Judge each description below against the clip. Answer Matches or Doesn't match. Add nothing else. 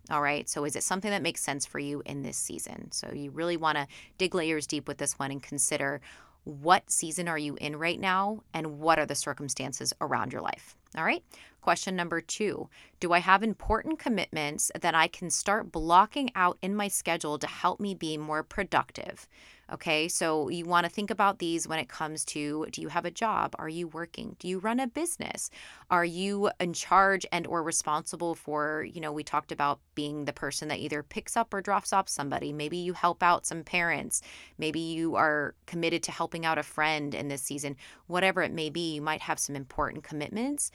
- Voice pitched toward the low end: Doesn't match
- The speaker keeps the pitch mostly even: Doesn't match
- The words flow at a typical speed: Doesn't match